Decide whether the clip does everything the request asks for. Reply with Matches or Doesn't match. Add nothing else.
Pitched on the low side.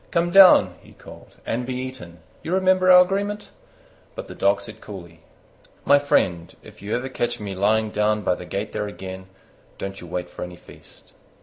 Matches